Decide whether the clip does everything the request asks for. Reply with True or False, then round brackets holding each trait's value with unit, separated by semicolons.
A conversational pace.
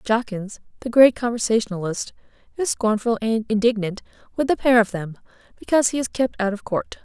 True (170 wpm)